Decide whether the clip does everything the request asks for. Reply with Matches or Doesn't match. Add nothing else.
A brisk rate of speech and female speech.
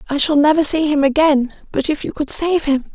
Matches